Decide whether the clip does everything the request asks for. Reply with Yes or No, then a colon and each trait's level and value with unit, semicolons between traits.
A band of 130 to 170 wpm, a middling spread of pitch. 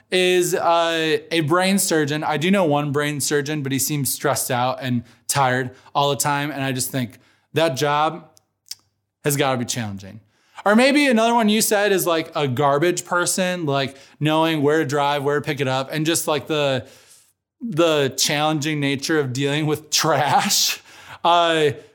No: average, 180 wpm; average, 3.5 semitones